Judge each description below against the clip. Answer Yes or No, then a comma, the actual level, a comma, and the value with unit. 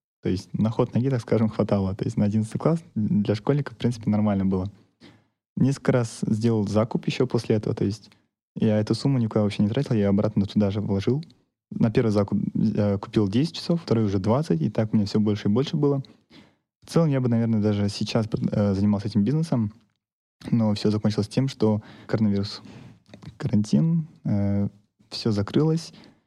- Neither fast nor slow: No, fast, 180 wpm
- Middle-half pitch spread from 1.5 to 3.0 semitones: No, average, 3.8 semitones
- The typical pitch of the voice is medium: No, low, 110 Hz